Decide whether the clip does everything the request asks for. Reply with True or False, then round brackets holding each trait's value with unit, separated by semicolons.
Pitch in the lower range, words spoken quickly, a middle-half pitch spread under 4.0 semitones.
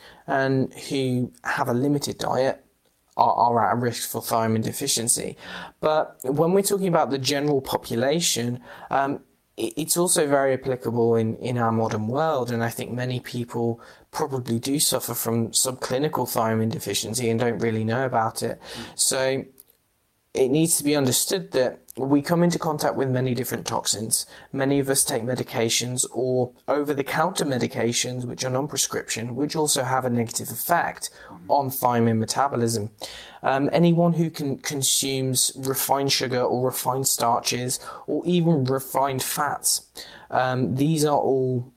False (130 Hz; 150 wpm; 3.0 semitones)